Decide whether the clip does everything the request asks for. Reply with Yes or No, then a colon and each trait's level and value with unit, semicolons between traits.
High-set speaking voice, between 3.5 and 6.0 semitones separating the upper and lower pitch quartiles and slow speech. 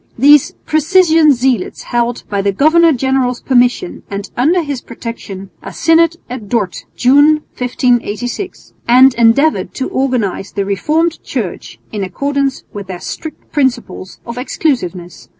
Yes: very high, 250 Hz; average, 5.1 semitones; slow, 130 wpm